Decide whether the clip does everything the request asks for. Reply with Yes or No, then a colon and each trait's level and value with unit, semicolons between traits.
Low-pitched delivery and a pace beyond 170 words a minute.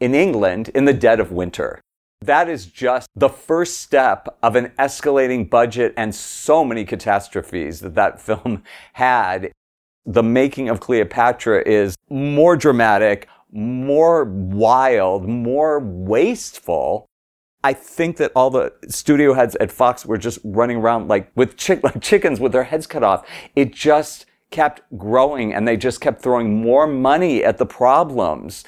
No: low, 125 Hz; average, 155 wpm